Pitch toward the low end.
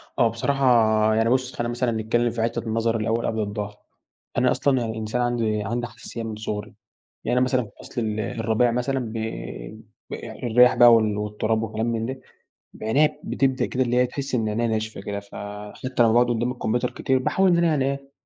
Yes: low, 115 Hz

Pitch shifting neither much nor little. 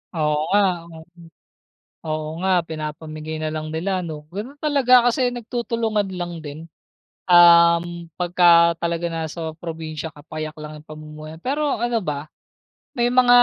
Yes: average, 4.9 semitones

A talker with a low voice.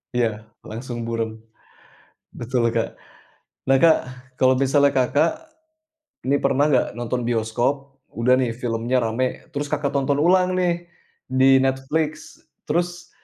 Yes: low, 130 Hz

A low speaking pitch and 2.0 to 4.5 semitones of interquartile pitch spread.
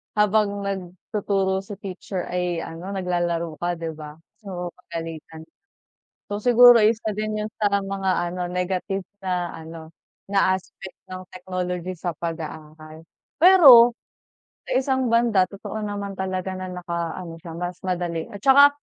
No: medium, 185 Hz; average, 3.0 semitones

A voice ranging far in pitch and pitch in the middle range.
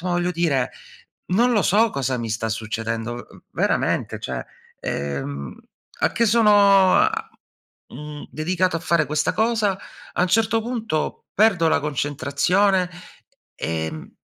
Yes: wide, 8.5 semitones; medium, 170 Hz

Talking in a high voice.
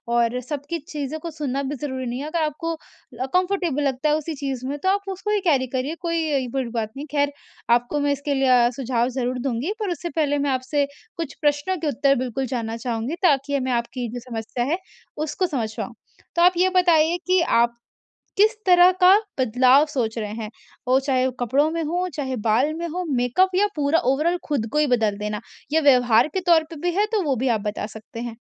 Yes: very high, 280 Hz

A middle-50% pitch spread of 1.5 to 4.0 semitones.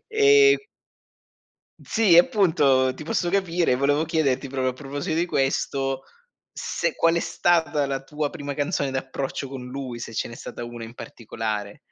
No: average, 4.4 semitones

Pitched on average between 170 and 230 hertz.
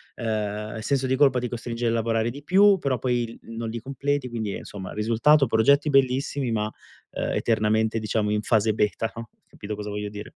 No: low, 115 Hz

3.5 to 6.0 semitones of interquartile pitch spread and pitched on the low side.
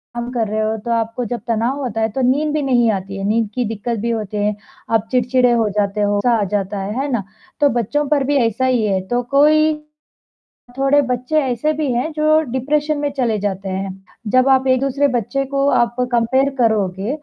No: average, 4.1 semitones; high, 240 Hz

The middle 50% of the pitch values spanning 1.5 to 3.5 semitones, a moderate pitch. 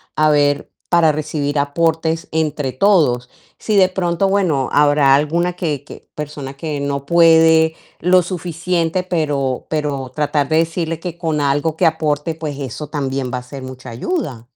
Yes: average, 2.7 semitones; medium, 155 Hz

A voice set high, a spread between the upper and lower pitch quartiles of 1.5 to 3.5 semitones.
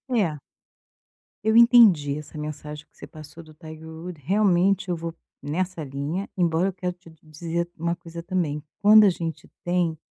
No: medium, 170 Hz; average, 3.0 semitones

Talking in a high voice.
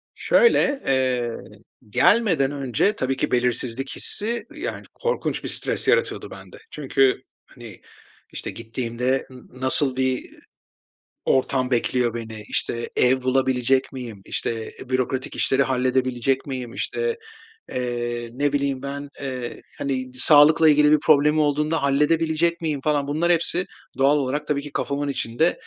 No: low, 135 Hz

